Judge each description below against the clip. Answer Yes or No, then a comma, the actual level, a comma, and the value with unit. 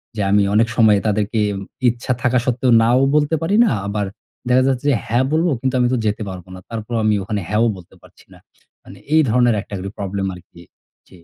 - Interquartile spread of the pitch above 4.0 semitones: No, average, 3.7 semitones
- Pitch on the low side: Yes, low, 115 Hz